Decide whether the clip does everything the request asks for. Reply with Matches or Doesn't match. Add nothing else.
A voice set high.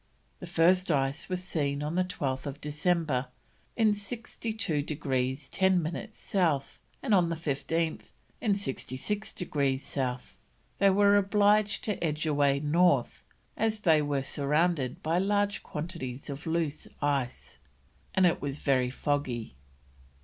Doesn't match